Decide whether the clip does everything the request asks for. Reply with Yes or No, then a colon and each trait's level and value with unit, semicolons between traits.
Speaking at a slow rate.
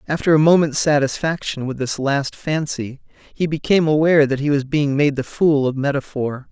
No: average, 185 wpm